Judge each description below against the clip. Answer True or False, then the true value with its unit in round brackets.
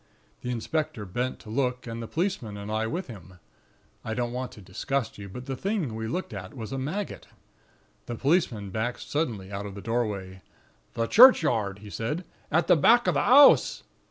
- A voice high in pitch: False (120 Hz)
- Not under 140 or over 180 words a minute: False (195 wpm)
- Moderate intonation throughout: False (6.0 semitones)